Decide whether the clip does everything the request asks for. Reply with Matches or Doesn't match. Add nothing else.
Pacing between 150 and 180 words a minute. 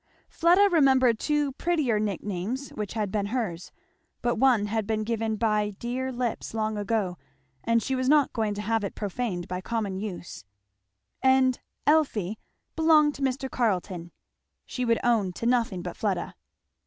Matches